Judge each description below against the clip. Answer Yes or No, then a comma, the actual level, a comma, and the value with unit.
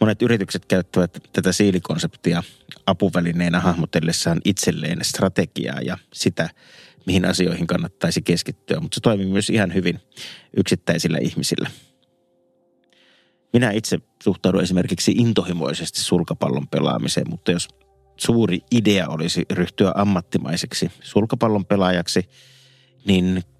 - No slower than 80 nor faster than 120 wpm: Yes, average, 100 wpm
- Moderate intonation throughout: Yes, average, 3.8 semitones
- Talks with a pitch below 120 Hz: Yes, very low, 95 Hz